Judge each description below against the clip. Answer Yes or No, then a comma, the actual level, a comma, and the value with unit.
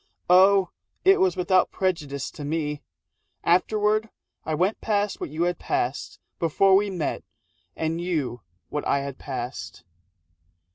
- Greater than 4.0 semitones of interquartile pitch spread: Yes, average, 5.0 semitones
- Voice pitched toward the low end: No, medium, 175 Hz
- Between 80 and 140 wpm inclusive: Yes, slow, 135 wpm